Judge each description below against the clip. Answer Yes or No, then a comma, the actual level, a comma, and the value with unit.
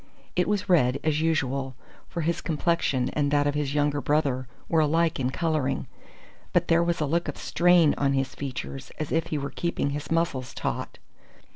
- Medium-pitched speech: Yes, medium, 150 Hz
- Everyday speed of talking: Yes, average, 185 wpm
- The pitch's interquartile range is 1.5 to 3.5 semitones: Yes, average, 3.2 semitones